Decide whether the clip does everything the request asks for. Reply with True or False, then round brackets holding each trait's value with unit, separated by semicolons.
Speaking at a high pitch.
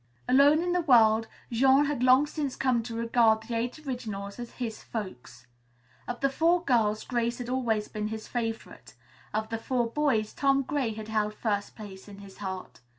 True (230 Hz)